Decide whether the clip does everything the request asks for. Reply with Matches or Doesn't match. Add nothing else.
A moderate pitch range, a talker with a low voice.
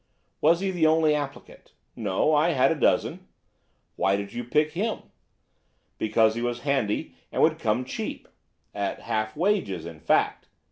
Doesn't match